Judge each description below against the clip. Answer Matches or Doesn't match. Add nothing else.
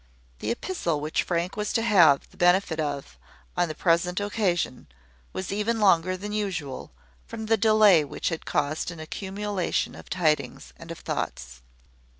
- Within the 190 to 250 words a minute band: Doesn't match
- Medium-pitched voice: Matches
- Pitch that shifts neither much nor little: Matches